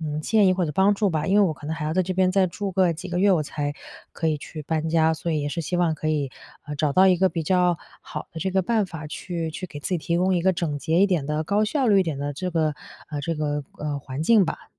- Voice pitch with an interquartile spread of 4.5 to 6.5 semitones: No, average, 3.5 semitones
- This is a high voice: No, medium, 165 Hz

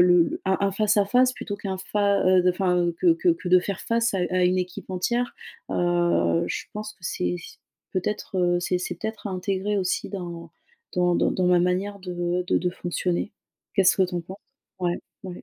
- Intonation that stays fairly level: Yes, narrow, 2.2 semitones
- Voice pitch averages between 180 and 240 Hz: Yes, medium, 185 Hz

